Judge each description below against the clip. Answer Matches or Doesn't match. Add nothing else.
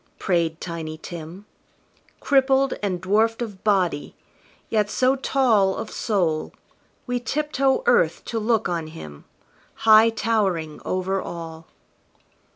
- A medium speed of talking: Doesn't match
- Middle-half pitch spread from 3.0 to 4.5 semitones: Doesn't match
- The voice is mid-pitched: Doesn't match